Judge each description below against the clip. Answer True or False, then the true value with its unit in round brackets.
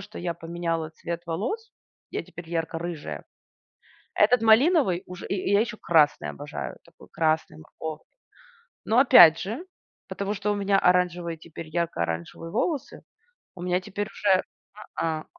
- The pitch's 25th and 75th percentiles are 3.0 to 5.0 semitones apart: True (4.0 semitones)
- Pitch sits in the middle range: True (175 Hz)